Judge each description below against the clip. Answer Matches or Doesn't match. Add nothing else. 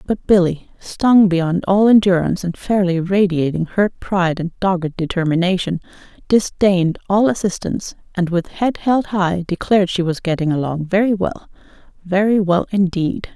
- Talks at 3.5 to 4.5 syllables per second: Doesn't match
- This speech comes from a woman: Matches